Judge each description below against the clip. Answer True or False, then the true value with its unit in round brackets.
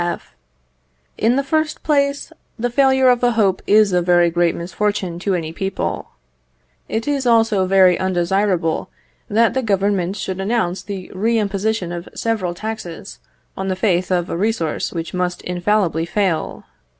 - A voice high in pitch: True (195 Hz)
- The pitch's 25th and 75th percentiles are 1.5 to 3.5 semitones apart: False (4.1 semitones)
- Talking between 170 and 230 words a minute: False (155 wpm)